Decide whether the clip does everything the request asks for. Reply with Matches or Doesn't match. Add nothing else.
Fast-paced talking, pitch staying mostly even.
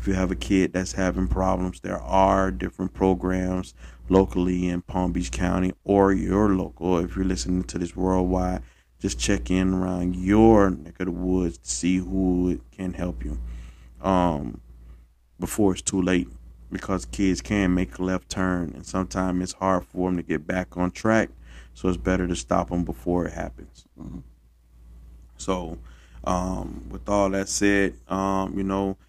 Doesn't match